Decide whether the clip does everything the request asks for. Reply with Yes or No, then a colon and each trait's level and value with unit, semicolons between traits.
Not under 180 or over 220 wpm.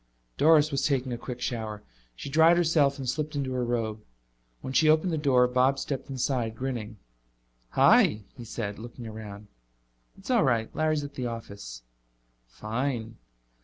No: average, 160 wpm